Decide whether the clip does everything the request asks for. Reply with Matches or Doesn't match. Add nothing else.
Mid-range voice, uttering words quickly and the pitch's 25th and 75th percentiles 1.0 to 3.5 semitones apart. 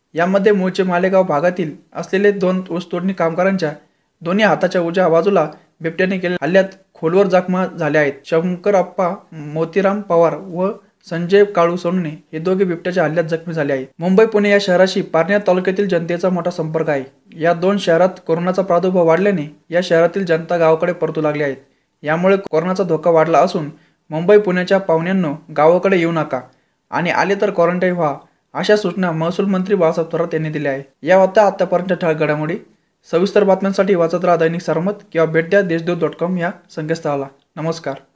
Matches